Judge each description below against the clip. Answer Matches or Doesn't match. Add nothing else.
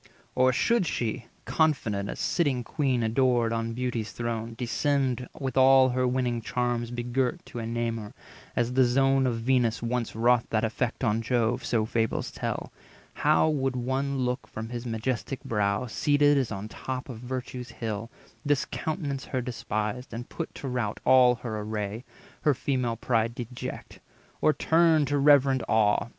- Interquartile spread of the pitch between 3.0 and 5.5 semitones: Doesn't match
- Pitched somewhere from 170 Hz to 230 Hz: Doesn't match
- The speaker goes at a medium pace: Matches